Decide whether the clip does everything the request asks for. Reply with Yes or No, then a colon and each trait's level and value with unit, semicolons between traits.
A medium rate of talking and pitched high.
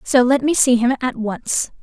No: fast, 230 wpm; very high, 250 Hz